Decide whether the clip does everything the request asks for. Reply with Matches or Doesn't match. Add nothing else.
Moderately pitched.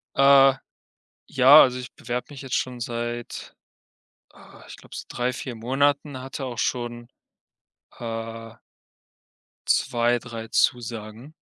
Doesn't match